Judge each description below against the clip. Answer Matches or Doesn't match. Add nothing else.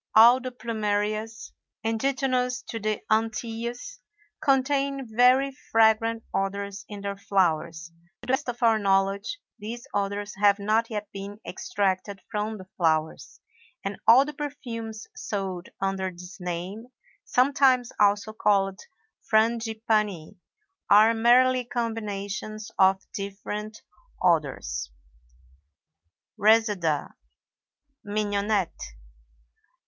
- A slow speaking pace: Matches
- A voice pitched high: Matches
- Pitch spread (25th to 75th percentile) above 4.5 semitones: Doesn't match